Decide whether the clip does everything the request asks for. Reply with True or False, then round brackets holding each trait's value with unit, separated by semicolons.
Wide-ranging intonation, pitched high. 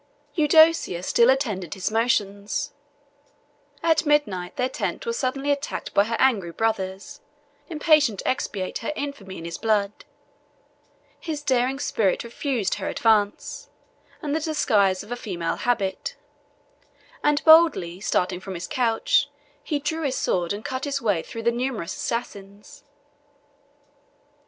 True (6.5 semitones; 230 Hz)